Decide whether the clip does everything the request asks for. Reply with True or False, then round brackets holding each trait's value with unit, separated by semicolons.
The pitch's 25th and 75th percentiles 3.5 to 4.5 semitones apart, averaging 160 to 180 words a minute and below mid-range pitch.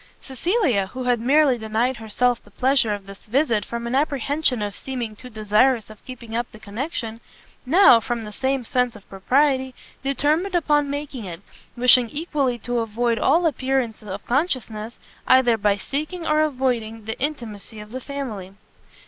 False (4.0 semitones; 165 wpm; 245 Hz)